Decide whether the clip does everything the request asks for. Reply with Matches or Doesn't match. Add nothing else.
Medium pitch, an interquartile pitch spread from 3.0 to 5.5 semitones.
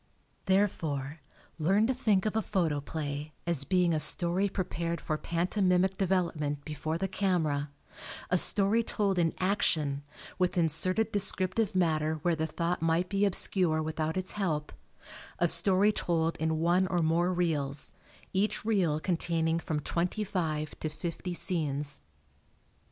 Matches